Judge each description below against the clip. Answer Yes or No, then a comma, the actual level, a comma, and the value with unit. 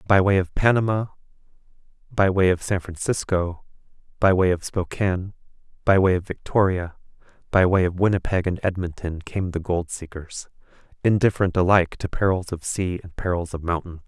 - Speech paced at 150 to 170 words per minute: Yes, average, 160 wpm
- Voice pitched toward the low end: Yes, very low, 90 Hz